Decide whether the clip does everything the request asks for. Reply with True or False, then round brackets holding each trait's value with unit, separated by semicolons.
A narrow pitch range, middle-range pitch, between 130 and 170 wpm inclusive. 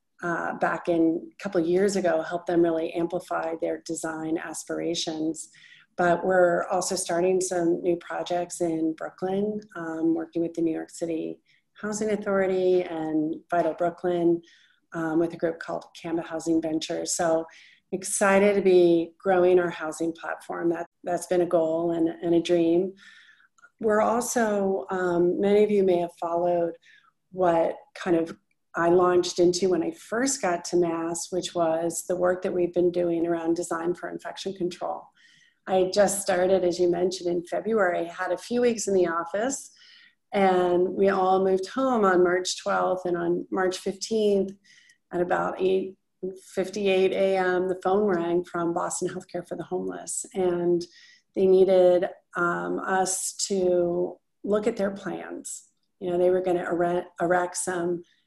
True (1.9 semitones; 180 Hz; 160 wpm)